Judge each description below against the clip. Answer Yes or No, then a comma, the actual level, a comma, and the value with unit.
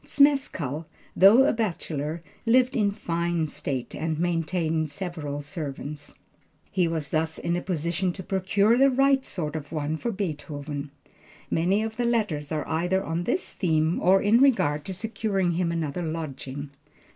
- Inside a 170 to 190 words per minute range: No, average, 155 wpm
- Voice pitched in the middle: Yes, medium, 170 Hz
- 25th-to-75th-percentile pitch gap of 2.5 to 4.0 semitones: No, average, 4.7 semitones